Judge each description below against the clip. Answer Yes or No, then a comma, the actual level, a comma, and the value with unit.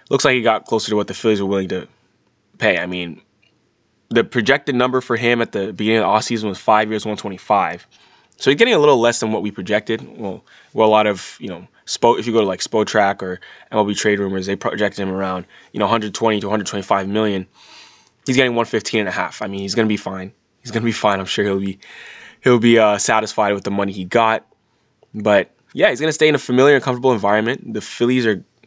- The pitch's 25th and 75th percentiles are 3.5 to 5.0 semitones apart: No, average, 2.8 semitones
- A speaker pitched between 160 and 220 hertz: No, low, 105 Hz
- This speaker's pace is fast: Yes, fast, 240 wpm